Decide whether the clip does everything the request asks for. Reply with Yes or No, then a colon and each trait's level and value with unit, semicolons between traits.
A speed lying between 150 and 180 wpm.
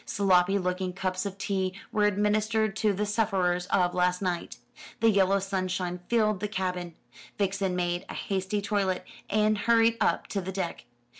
Yes: average, 160 wpm